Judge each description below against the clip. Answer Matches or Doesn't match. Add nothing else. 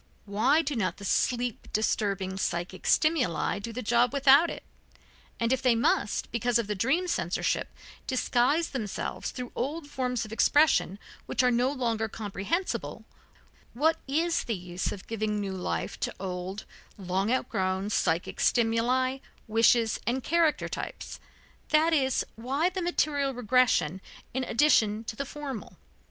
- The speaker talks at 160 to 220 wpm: Doesn't match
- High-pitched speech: Matches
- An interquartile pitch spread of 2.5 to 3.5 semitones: Doesn't match